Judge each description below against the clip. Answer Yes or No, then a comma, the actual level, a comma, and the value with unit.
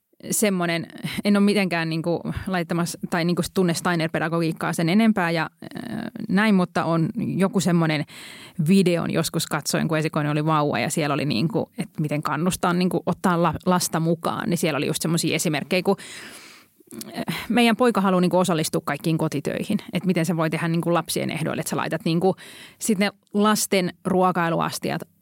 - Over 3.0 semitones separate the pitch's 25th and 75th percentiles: No, average, 2.7 semitones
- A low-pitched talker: No, medium, 175 Hz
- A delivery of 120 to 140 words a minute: No, fast, 155 wpm